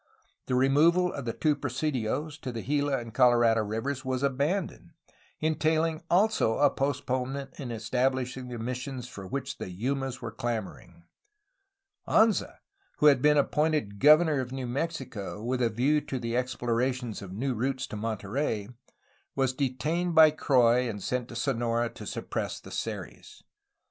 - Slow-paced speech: No, average, 155 wpm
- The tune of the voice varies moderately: Yes, average, 3.5 semitones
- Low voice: Yes, low, 130 Hz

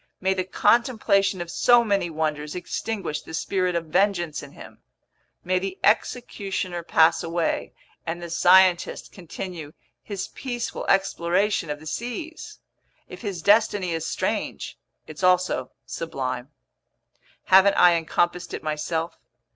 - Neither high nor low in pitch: Yes, medium, 180 Hz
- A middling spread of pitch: Yes, average, 3.3 semitones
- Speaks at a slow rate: Yes, slow, 130 wpm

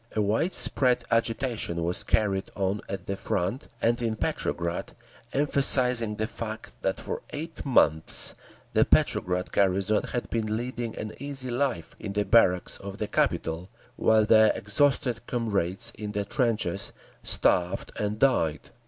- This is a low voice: Yes, low, 110 Hz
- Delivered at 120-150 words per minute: Yes, average, 145 wpm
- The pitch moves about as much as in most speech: Yes, average, 3.9 semitones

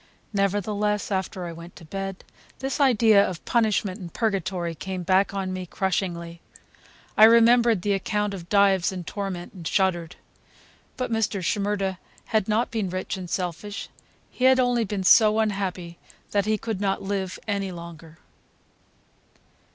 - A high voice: Yes, high, 195 Hz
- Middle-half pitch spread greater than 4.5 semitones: No, average, 2.7 semitones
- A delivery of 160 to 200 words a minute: No, average, 150 wpm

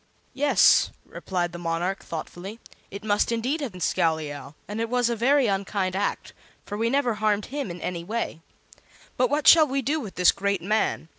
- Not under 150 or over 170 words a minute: No, average, 190 wpm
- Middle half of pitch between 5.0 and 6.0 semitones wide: Yes, wide, 5.4 semitones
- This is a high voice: Yes, high, 210 Hz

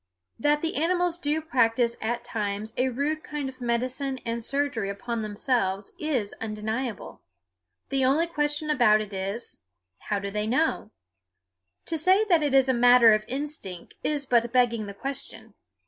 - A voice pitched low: No, high, 245 Hz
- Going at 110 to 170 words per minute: Yes, average, 155 wpm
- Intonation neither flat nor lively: Yes, average, 5.0 semitones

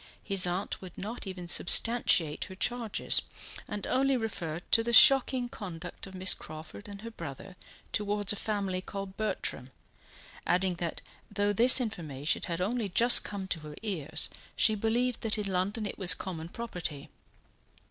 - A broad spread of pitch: No, average, 3.9 semitones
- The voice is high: Yes, high, 195 Hz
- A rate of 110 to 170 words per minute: Yes, average, 160 wpm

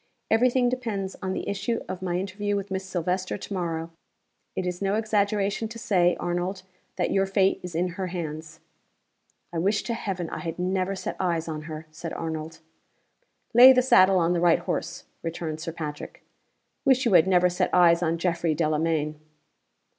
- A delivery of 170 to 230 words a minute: Yes, average, 180 wpm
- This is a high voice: No, medium, 180 Hz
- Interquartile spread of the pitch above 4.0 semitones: No, average, 3.1 semitones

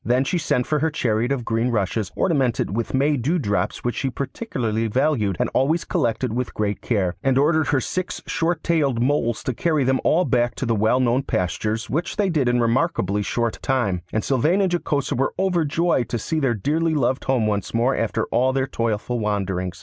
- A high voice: No, low, 125 Hz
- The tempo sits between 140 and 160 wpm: No, fast, 205 wpm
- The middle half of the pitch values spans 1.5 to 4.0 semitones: No, average, 4.8 semitones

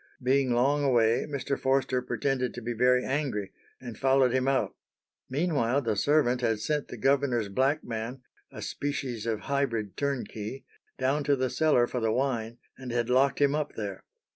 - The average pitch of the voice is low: Yes, low, 130 Hz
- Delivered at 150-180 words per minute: Yes, average, 170 wpm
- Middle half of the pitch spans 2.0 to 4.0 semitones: Yes, average, 2.9 semitones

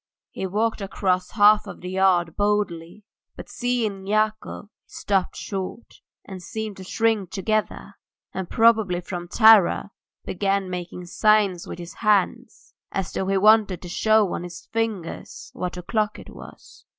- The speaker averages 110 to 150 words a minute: Yes, average, 145 wpm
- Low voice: No, high, 195 Hz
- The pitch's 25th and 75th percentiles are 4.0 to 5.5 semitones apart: No, average, 3.0 semitones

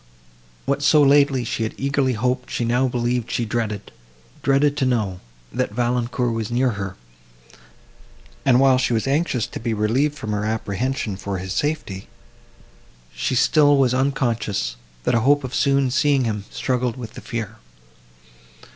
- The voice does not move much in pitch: No, average, 3.7 semitones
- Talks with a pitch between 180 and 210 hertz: No, low, 125 Hz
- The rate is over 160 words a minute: No, average, 155 wpm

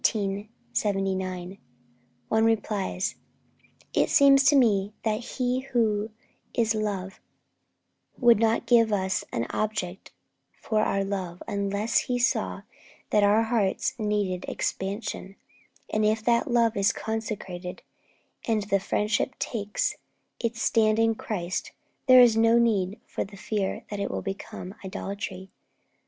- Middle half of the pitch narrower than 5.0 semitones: Yes, narrow, 2.6 semitones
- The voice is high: Yes, high, 215 Hz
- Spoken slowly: Yes, slow, 125 wpm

